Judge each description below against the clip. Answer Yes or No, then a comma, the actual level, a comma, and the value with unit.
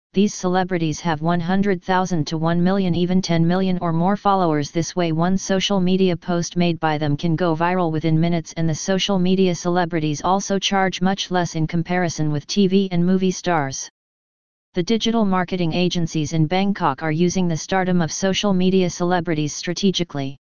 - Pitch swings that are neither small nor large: No, narrow, 2.3 semitones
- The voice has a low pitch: No, medium, 175 Hz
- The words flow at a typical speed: Yes, average, 170 wpm